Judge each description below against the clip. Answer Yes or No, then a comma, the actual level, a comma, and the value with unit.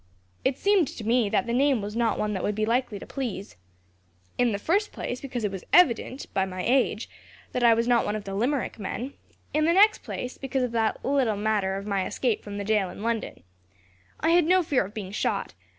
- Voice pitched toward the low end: No, high, 235 Hz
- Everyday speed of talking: No, fast, 230 wpm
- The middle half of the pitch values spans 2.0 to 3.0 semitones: No, average, 4.4 semitones